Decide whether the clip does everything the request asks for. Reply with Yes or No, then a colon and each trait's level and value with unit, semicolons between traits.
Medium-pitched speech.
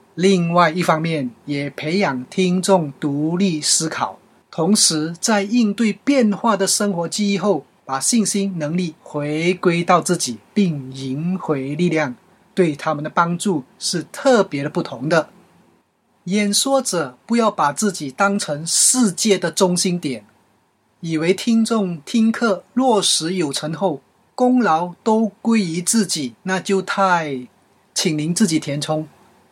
Yes: medium, 180 Hz